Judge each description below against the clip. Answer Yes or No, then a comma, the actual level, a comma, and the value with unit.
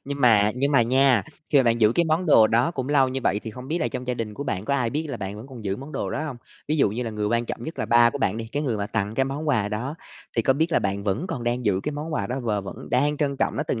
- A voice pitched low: Yes, low, 125 Hz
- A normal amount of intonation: Yes, average, 4.6 semitones